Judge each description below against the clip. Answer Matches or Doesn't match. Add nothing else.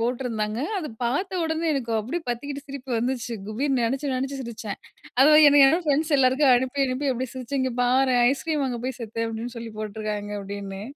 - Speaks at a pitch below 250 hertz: Doesn't match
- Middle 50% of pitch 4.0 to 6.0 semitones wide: Doesn't match